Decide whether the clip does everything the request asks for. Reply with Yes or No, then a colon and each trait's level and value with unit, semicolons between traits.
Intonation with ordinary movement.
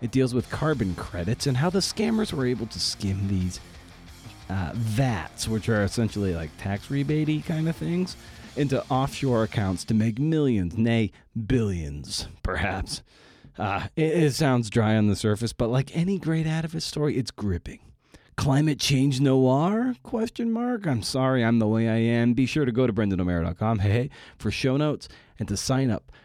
No: wide, 5.8 semitones